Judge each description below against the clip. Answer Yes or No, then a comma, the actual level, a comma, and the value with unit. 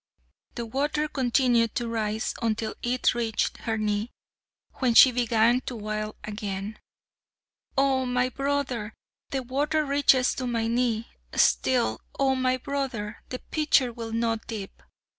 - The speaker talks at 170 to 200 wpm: No, slow, 135 wpm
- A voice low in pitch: No, high, 240 Hz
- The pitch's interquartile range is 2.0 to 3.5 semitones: Yes, average, 2.8 semitones